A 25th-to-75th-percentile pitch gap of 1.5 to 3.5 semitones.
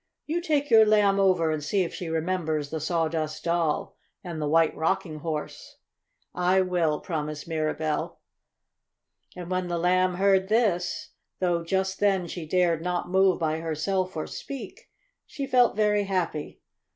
Yes: average, 3.1 semitones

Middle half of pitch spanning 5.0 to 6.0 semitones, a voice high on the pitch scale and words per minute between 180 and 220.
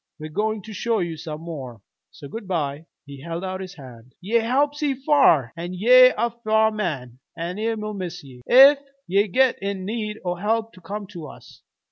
Yes: wide, 5.5 semitones; high, 195 Hz; average, 190 wpm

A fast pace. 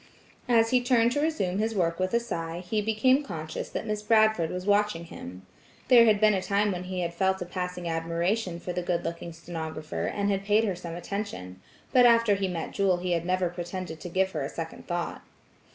Yes: fast, 215 wpm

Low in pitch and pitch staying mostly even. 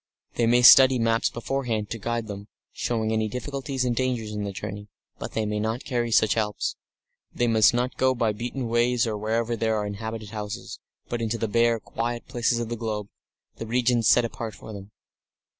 Yes: low, 115 Hz; narrow, 1.8 semitones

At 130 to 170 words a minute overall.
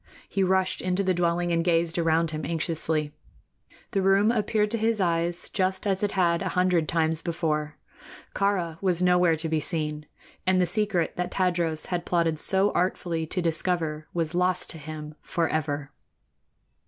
Yes: average, 165 wpm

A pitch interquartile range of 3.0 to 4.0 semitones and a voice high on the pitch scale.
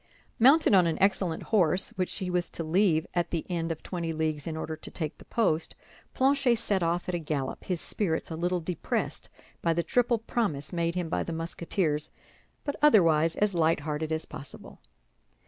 No: average, 3.3 semitones; medium, 170 Hz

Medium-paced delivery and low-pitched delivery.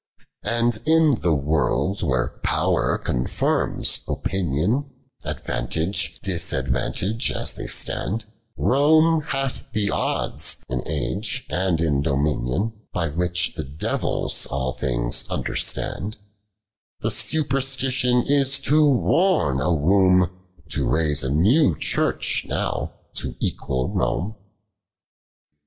No: slow, 105 wpm; very low, 95 Hz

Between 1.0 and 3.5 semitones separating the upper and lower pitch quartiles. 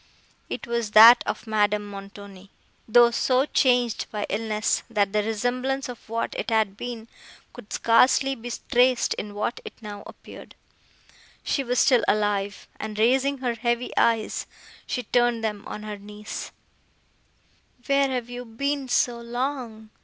Yes: average, 2.8 semitones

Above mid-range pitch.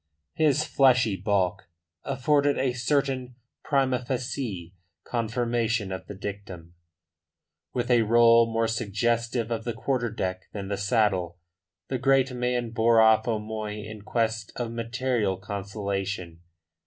No: low, 115 Hz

